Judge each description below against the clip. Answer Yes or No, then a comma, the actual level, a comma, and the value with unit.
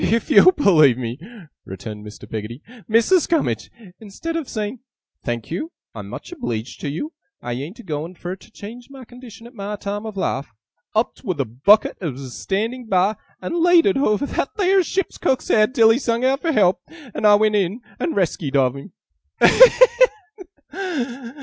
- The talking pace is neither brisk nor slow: Yes, average, 180 wpm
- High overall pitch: Yes, high, 210 Hz